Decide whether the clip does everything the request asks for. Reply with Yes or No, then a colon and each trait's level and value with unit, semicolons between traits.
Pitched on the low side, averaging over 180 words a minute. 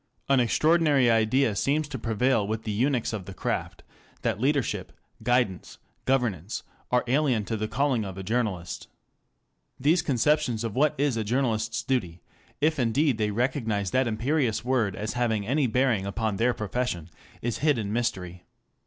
No: low, 120 Hz; average, 160 wpm